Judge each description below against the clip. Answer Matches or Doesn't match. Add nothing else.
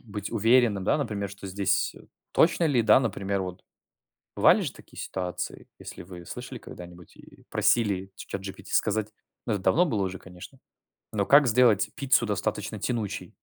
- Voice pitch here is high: Doesn't match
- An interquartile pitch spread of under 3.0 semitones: Doesn't match